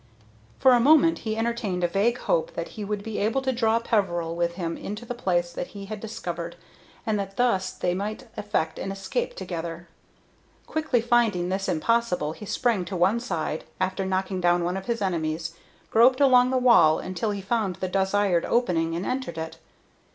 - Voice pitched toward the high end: Yes, high, 195 Hz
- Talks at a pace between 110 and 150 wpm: No, average, 190 wpm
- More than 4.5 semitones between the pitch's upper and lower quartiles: Yes, average, 5.1 semitones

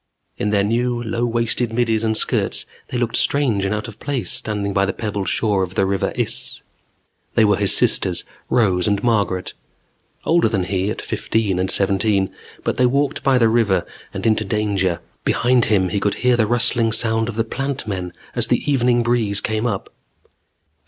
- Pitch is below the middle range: Yes, low, 110 Hz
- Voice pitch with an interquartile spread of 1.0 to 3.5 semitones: Yes, average, 3.2 semitones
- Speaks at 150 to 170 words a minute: No, average, 185 wpm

